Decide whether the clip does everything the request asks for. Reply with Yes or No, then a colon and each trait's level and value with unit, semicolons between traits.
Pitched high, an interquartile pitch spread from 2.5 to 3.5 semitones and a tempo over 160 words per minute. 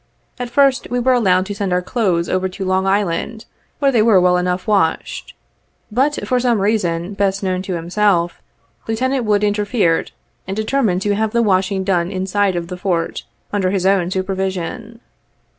Yes: high, 195 Hz; average, 3.2 semitones; average, 175 wpm